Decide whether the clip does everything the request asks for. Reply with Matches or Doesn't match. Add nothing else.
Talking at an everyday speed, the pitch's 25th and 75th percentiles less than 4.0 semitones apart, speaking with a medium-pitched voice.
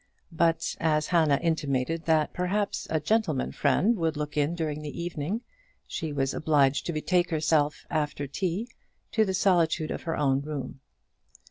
Matches